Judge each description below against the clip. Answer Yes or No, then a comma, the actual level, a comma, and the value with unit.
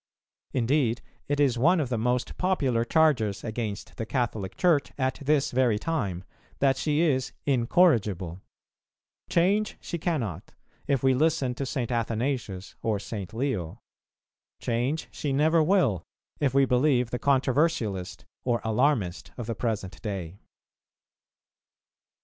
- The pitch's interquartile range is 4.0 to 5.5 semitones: Yes, average, 4.7 semitones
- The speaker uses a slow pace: Yes, slow, 130 wpm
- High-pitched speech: No, low, 125 Hz